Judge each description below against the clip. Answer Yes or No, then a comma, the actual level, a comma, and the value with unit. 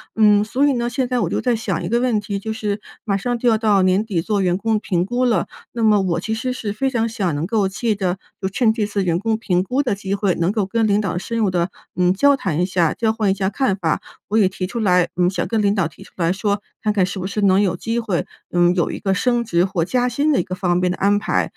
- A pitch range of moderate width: Yes, average, 3.6 semitones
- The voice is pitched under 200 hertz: No, high, 205 Hz